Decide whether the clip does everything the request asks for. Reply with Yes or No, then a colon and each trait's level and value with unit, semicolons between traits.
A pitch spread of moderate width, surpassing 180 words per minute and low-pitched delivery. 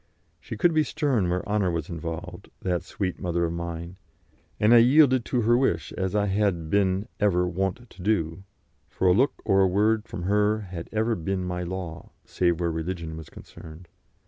Yes: average, 3.7 semitones; average, 190 wpm; very low, 95 Hz